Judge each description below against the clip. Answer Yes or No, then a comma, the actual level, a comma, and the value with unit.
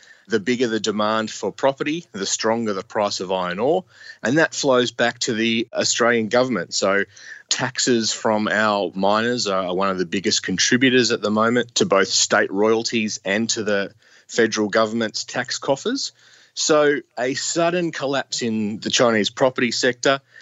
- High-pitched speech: No, low, 115 Hz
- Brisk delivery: No, average, 160 wpm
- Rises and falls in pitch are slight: No, average, 3.1 semitones